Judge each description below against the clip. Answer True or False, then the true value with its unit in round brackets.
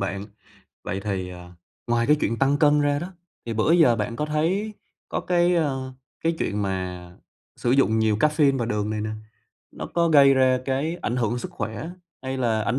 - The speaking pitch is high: False (130 Hz)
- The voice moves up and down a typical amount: False (5.8 semitones)